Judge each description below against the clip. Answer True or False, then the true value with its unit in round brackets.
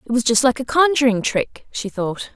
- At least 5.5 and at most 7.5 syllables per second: False (5.0 syllables/s)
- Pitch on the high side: True (240 Hz)